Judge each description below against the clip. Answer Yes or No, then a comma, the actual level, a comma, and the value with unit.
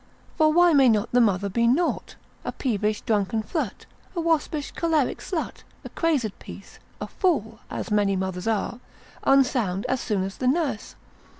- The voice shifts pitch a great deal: Yes, wide, 6.8 semitones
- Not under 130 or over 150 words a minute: No, average, 165 wpm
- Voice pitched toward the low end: No, high, 240 Hz